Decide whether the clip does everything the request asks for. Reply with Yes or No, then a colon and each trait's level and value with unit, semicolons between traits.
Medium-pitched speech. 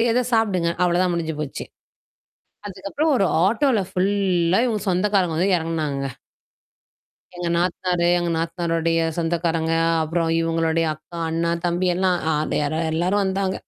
Yes: medium, 175 Hz